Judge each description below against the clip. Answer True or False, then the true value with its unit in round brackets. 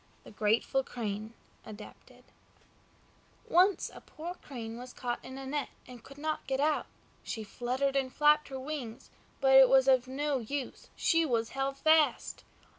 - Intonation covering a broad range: False (3.2 semitones)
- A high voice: True (265 Hz)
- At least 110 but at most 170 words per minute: True (160 wpm)